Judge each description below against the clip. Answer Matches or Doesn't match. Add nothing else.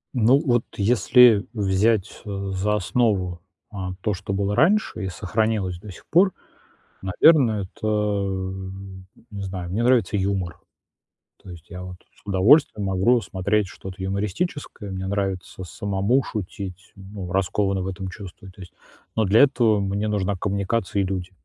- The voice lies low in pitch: Matches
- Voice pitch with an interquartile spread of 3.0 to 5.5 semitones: Doesn't match